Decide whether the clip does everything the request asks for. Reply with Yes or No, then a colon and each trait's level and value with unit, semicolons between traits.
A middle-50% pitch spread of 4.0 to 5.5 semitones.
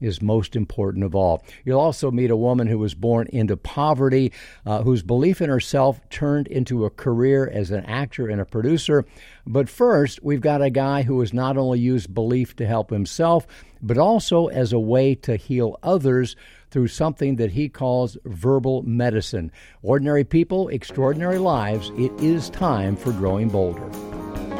Yes: average, 4.3 semitones